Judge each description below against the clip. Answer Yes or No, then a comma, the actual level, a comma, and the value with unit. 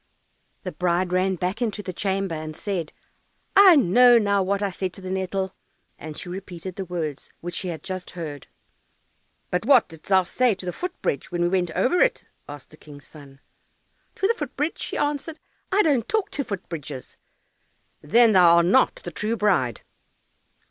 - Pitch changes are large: No, average, 5.0 semitones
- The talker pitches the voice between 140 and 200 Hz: Yes, medium, 185 Hz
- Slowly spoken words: No, average, 190 wpm